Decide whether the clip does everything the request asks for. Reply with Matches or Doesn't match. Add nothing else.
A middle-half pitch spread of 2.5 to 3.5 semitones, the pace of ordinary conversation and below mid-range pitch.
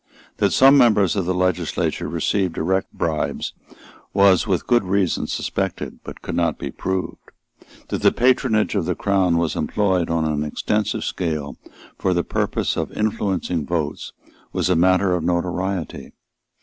Matches